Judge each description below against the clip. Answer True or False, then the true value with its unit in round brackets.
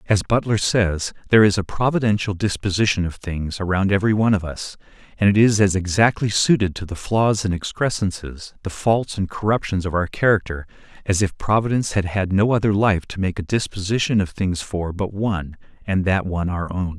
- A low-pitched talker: True (100 Hz)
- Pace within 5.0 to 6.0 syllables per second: True (5.6 syllables/s)